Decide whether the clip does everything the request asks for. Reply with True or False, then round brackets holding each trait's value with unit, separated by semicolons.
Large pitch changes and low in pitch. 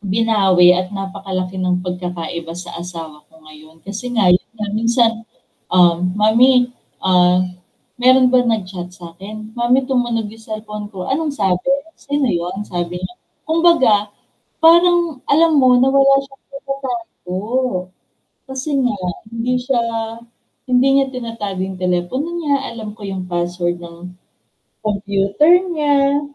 False (6.1 semitones; 215 Hz)